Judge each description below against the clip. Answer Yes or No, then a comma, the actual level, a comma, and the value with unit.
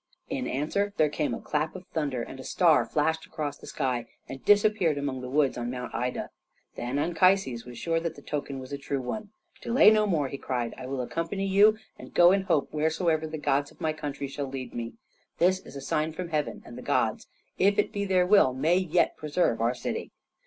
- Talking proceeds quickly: Yes, fast, 220 wpm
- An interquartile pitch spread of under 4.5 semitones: No, average, 5.1 semitones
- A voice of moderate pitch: Yes, medium, 150 Hz